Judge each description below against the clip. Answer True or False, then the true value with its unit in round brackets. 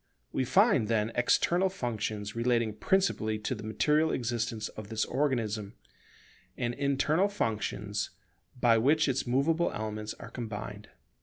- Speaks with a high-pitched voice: False (115 Hz)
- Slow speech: True (130 wpm)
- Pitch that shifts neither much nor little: True (4.3 semitones)